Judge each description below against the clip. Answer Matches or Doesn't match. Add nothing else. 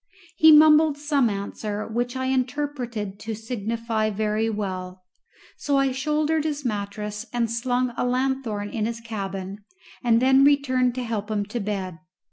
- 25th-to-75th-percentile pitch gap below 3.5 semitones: Doesn't match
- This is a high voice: Matches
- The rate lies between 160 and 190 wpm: Doesn't match